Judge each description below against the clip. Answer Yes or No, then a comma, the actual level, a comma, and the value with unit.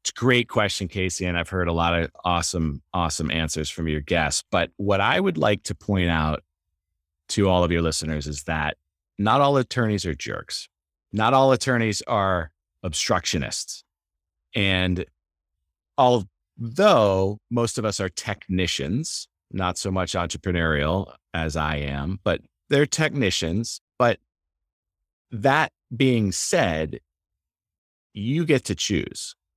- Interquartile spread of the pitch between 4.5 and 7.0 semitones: Yes, average, 4.9 semitones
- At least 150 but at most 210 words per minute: No, slow, 135 wpm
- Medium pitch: No, very low, 90 Hz